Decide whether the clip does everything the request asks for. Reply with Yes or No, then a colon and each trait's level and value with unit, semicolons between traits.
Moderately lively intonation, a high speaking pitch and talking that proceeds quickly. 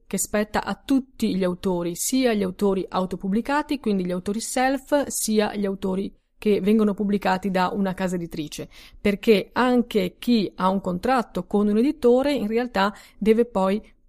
No: average, 3.8 semitones; high, 205 Hz; average, 160 wpm